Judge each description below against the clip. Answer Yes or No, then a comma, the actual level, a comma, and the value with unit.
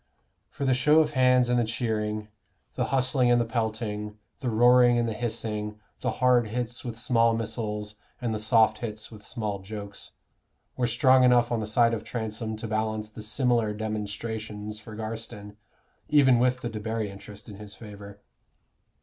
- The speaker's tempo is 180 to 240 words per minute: No, average, 170 wpm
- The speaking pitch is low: Yes, low, 110 Hz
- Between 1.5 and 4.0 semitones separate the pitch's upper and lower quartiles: Yes, narrow, 2.4 semitones